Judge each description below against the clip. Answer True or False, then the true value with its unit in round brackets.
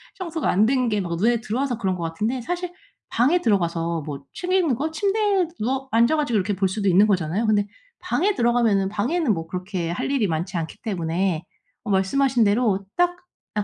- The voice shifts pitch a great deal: True (6.5 semitones)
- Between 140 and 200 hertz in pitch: False (215 Hz)